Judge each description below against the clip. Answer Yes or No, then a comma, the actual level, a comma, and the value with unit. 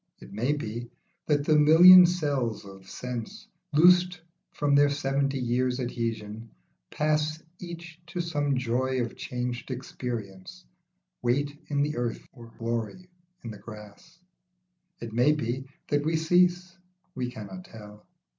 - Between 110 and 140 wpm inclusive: Yes, slow, 135 wpm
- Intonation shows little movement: No, average, 4.7 semitones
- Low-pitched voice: Yes, low, 130 Hz